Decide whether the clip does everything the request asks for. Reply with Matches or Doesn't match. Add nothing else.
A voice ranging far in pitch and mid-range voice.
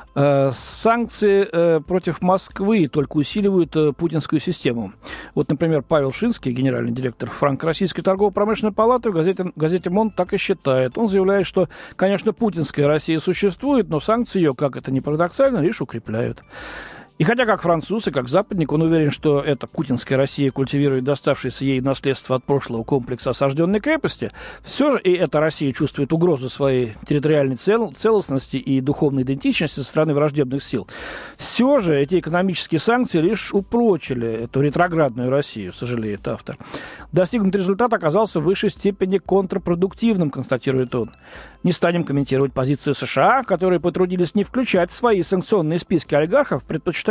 Matches